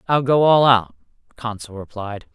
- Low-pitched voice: Yes, low, 115 Hz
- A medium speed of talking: Yes, average, 155 wpm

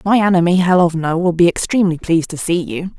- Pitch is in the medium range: Yes, medium, 175 Hz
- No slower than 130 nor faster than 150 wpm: No, average, 200 wpm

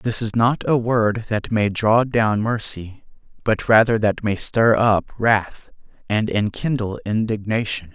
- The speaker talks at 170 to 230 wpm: No, average, 150 wpm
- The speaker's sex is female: No, male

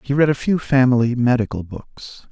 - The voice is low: Yes, low, 125 Hz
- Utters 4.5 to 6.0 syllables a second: Yes, 5.1 syllables/s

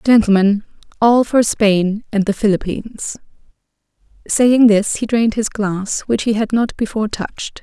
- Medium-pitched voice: No, high, 215 Hz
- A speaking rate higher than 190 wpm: No, average, 150 wpm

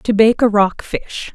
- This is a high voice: Yes, high, 215 Hz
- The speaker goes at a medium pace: No, fast, 225 wpm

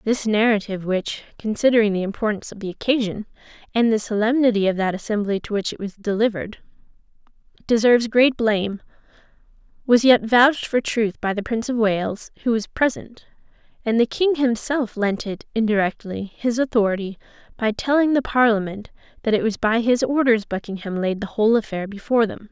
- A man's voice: No, female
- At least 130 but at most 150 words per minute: No, average, 165 wpm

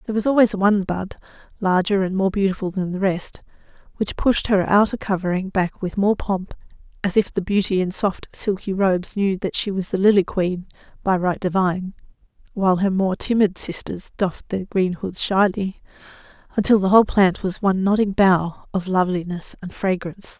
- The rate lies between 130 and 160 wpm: No, average, 180 wpm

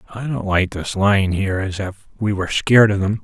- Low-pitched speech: Yes, low, 100 Hz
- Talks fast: Yes, fast, 240 wpm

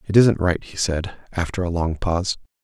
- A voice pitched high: No, very low, 90 Hz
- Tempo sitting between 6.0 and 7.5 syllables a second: No, 5.1 syllables/s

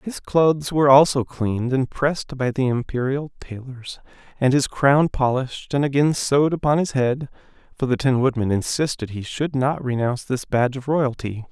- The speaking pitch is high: No, low, 135 Hz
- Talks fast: No, average, 175 wpm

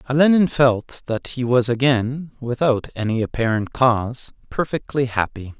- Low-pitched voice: Yes, low, 125 Hz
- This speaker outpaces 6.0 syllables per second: No, 4.5 syllables/s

